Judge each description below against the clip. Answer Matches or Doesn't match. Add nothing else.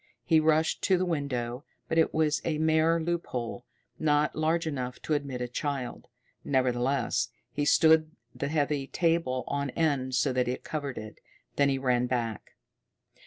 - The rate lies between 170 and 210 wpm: Doesn't match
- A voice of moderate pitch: Matches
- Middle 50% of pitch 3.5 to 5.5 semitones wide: Matches